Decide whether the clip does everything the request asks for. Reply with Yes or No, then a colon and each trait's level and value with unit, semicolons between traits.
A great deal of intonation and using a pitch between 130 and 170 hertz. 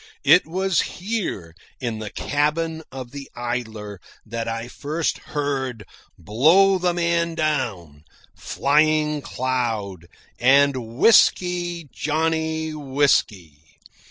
Yes: wide, 5.9 semitones; medium, 140 Hz